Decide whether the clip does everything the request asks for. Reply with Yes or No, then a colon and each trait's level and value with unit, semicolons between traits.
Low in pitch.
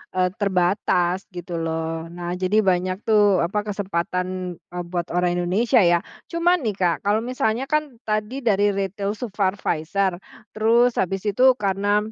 No: high, 195 Hz